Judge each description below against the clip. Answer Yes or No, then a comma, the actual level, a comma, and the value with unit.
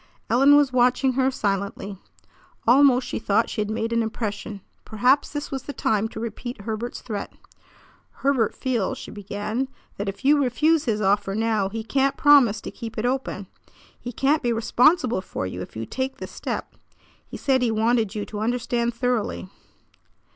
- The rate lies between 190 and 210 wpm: No, average, 175 wpm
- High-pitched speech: Yes, high, 235 Hz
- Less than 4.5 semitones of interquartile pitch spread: Yes, average, 3.8 semitones